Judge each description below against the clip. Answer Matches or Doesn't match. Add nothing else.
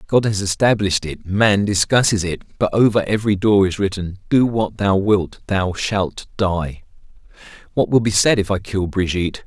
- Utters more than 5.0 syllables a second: Doesn't match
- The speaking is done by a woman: Doesn't match